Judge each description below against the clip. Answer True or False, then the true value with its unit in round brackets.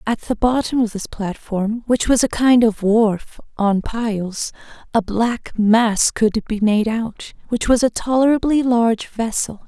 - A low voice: False (225 Hz)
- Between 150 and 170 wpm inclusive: True (165 wpm)